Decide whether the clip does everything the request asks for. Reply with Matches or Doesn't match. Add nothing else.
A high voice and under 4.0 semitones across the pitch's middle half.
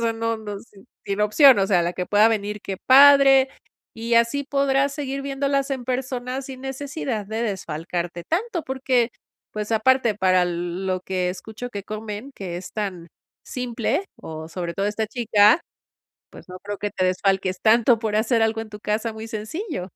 Doesn't match